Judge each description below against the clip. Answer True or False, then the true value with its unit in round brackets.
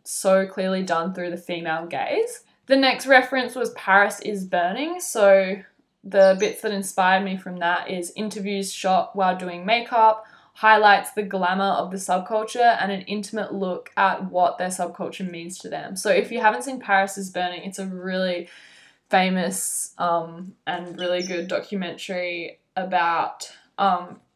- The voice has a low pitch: False (190 Hz)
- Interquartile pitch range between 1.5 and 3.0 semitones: True (2.6 semitones)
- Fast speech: False (160 wpm)